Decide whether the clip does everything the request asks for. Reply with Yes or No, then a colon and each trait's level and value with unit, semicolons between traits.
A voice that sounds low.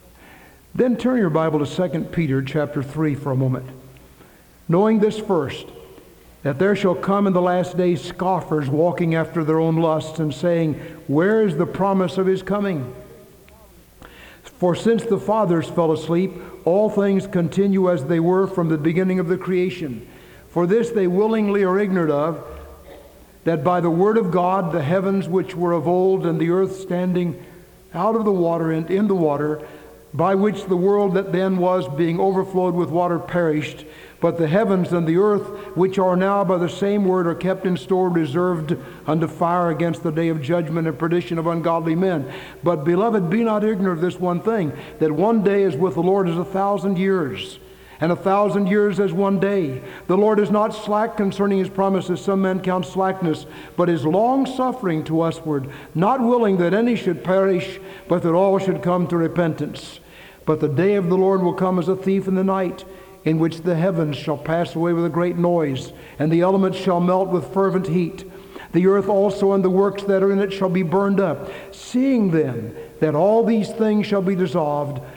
No: medium, 180 Hz